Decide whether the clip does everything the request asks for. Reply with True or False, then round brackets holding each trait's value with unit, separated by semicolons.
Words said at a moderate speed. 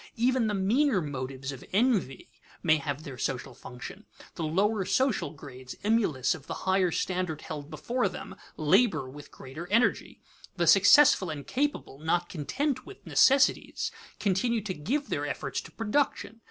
True (155 wpm)